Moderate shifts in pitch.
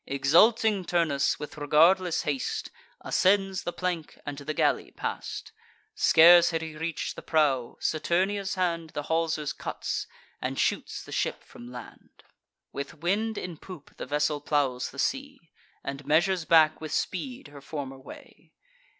Yes: average, 3.9 semitones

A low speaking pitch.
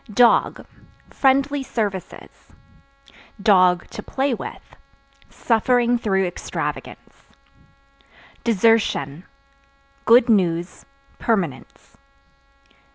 No: high, 225 Hz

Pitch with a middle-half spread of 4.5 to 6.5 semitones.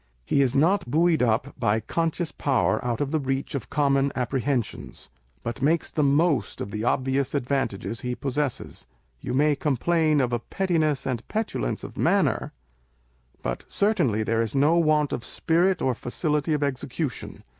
No: average, 4.0 semitones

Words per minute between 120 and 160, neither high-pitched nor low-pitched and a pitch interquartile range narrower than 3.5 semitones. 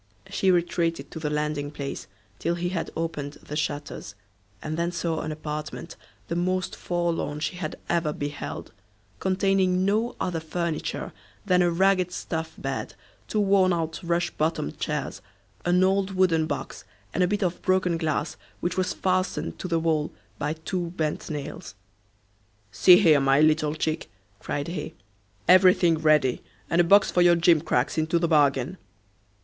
Yes: average, 155 wpm; medium, 170 Hz; average, 3.0 semitones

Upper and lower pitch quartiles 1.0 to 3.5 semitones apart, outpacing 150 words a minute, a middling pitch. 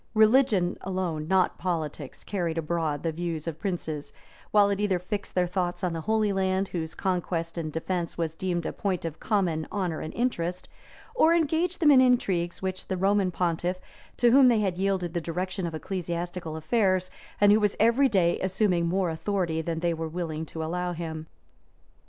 Yes: average, 3.1 semitones; average, 180 wpm; medium, 180 Hz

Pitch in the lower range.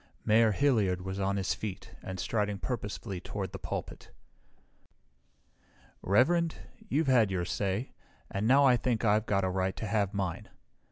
Yes: low, 105 Hz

